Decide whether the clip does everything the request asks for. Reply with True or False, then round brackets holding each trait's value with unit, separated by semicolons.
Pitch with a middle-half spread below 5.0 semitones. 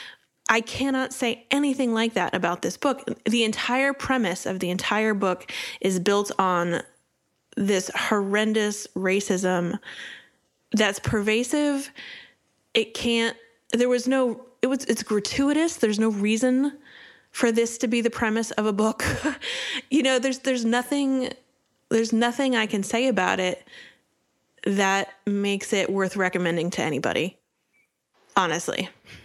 True (4.1 semitones)